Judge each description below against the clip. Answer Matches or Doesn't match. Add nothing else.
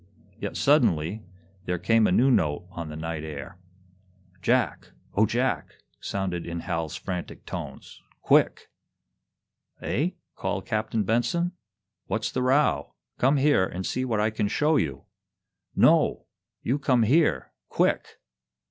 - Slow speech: Matches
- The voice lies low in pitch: Matches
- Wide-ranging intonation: Matches